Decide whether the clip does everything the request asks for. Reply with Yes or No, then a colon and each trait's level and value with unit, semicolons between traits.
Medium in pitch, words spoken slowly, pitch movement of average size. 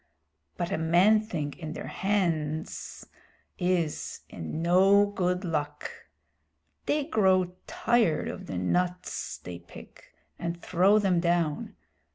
Yes: medium, 175 Hz; slow, 120 wpm; average, 3.5 semitones